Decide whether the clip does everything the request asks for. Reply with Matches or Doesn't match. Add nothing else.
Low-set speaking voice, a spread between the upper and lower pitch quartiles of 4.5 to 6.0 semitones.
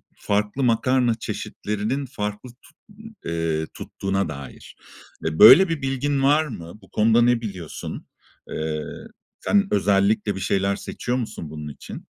Matches